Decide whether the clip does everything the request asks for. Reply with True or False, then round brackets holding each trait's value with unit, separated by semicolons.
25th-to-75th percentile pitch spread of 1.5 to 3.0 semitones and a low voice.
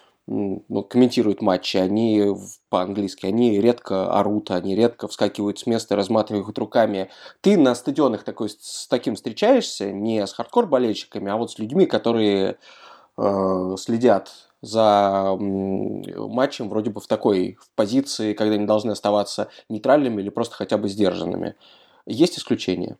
True (2.5 semitones; 105 Hz)